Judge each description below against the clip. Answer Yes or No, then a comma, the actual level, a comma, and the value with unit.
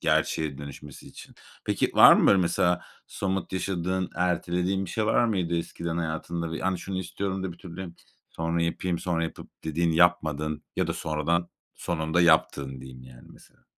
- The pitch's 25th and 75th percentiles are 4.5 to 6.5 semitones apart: No, narrow, 2.6 semitones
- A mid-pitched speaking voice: No, very low, 85 Hz